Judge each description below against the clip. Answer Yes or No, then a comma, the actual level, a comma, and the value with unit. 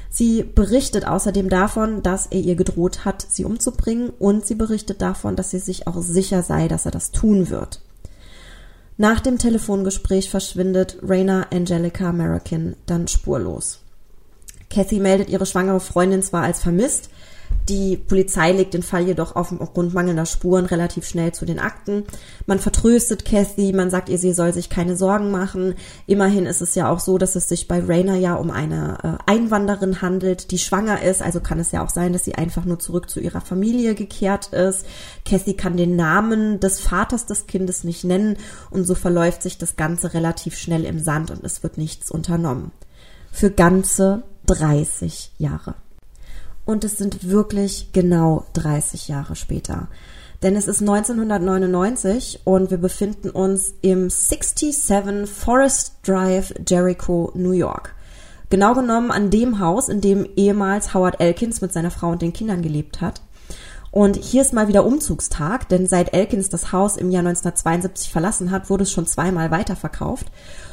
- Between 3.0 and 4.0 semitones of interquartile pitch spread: No, narrow, 2.4 semitones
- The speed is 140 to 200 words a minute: Yes, average, 165 wpm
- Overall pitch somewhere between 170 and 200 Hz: Yes, medium, 185 Hz